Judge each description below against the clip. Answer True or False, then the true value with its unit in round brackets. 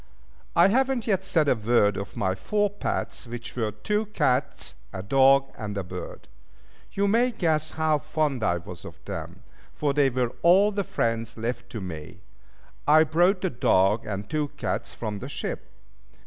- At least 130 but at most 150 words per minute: False (175 wpm)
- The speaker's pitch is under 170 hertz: True (135 Hz)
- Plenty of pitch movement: True (8.4 semitones)